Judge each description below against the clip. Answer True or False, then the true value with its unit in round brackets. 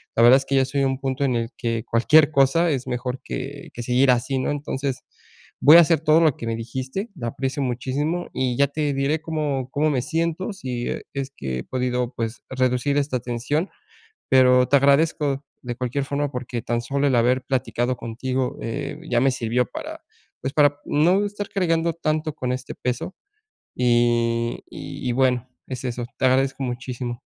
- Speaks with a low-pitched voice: True (130 Hz)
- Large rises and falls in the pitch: False (2.8 semitones)